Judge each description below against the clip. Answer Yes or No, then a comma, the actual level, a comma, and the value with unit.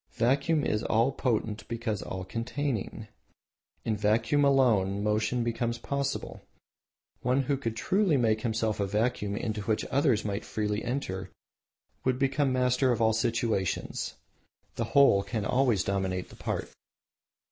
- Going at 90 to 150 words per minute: Yes, slow, 135 wpm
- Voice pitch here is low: Yes, low, 115 Hz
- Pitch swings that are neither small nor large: Yes, average, 3.6 semitones